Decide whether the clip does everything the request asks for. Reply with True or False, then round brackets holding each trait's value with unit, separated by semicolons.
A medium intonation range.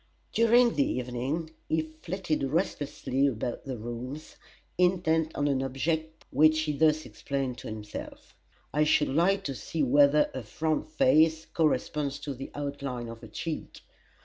True (3.2 semitones)